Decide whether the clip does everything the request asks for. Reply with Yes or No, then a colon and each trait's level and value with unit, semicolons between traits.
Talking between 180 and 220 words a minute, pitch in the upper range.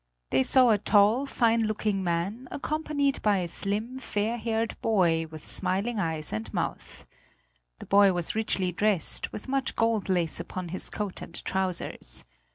No: average, 160 wpm; high, 205 Hz